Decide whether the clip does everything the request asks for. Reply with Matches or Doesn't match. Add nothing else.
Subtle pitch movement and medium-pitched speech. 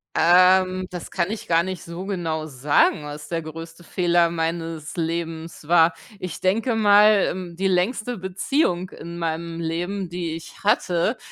Matches